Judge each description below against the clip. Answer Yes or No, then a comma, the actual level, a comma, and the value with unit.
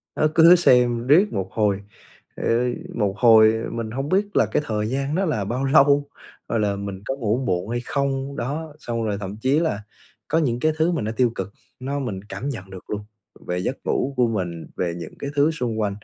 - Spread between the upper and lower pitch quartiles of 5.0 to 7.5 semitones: Yes, wide, 5.4 semitones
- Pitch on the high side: No, low, 120 Hz